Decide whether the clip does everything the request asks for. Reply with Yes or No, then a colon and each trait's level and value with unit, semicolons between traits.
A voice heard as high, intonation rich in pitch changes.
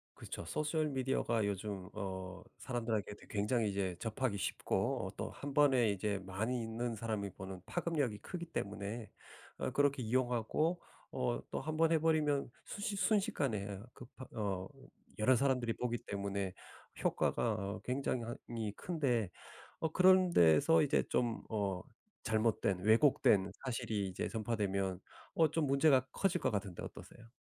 No: low, 115 Hz; wide, 5.7 semitones